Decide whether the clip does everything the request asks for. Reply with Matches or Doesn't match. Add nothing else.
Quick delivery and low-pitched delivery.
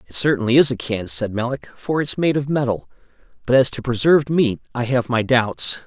Matches